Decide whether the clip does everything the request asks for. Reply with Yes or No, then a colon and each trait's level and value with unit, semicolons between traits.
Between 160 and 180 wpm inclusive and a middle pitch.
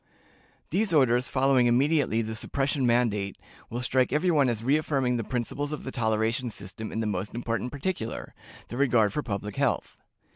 No: average, 170 wpm; low, 125 Hz